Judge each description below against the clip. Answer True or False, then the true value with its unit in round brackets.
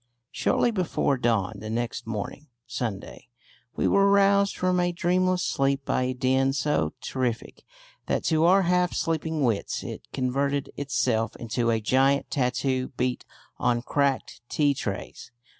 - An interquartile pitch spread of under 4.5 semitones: False (5.5 semitones)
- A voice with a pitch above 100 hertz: True (135 Hz)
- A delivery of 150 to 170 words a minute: False (140 wpm)